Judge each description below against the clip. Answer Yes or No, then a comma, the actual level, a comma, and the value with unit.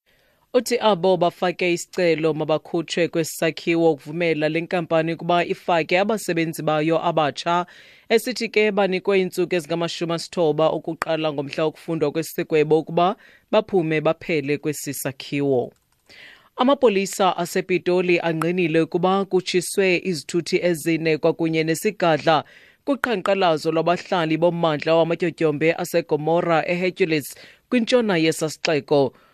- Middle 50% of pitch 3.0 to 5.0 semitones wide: No, narrow, 2.5 semitones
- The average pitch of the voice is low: No, medium, 170 Hz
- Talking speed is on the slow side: Yes, slow, 90 wpm